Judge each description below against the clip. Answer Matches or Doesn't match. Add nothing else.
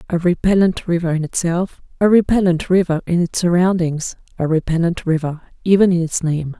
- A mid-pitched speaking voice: Matches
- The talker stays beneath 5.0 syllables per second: Doesn't match